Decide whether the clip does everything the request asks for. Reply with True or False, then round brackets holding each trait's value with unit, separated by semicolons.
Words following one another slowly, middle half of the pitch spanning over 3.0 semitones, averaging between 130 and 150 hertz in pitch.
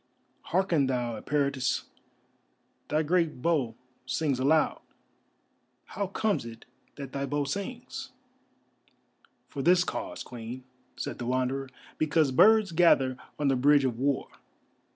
True (120 wpm; 4.6 semitones; 140 Hz)